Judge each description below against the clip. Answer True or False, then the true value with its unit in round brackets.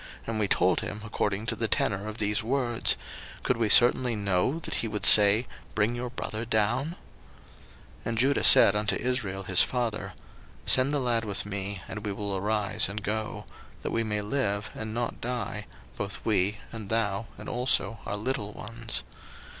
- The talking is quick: False (180 wpm)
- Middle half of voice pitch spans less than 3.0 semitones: True (2.5 semitones)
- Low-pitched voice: True (110 Hz)